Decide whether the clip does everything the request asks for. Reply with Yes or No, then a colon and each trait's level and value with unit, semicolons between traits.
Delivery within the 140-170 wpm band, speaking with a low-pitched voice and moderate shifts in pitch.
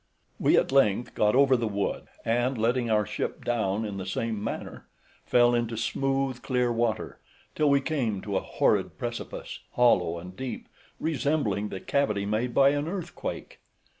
Yes: average, 165 wpm; low, 120 Hz; average, 4.3 semitones